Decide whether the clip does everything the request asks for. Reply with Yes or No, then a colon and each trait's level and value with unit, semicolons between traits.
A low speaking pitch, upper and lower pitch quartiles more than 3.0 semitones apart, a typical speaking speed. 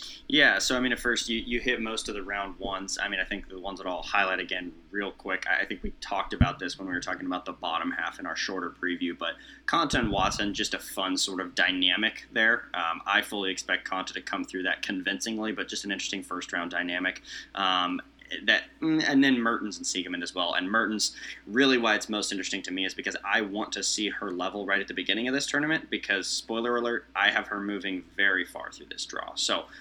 No: low, 100 Hz; average, 3.8 semitones; fast, 240 wpm